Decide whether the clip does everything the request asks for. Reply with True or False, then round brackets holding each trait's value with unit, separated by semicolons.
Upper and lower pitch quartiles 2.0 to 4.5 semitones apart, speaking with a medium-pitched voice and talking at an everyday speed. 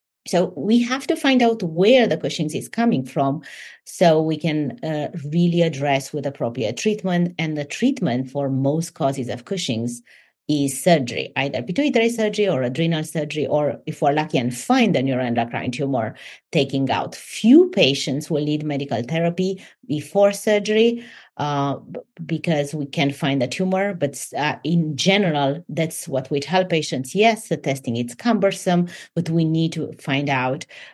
False (5.3 semitones; 155 Hz; 160 wpm)